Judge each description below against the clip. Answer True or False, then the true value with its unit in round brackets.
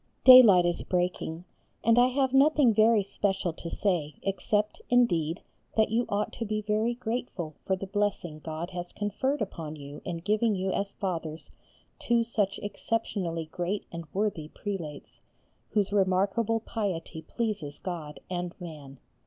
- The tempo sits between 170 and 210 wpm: False (145 wpm)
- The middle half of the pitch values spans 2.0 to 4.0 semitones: False (4.4 semitones)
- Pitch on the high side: True (195 Hz)